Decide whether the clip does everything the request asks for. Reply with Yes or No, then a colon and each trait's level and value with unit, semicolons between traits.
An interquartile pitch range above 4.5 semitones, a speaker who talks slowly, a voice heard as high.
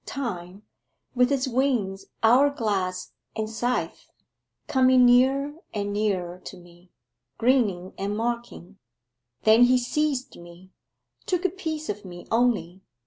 Yes: average, 5.2 semitones; slow, 125 wpm; high, 225 Hz